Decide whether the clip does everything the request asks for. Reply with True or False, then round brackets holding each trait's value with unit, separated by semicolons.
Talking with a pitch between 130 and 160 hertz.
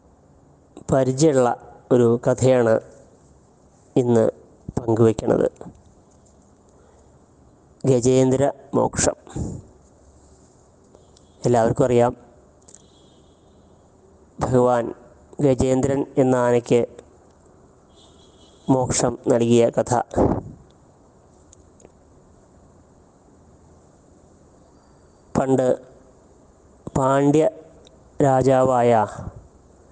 False (115 Hz)